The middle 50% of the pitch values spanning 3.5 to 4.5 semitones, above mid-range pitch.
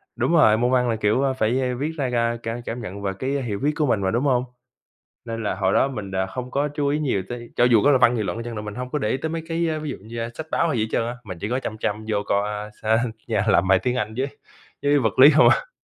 No: average, 4.2 semitones; low, 120 Hz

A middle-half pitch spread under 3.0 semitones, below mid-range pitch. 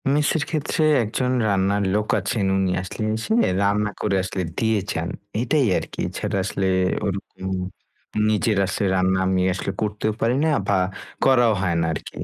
No: average, 3.3 semitones; low, 105 Hz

